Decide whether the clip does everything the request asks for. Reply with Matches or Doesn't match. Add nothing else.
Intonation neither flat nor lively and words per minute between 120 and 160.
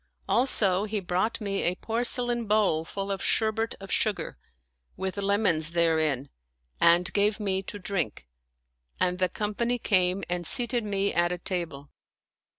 Matches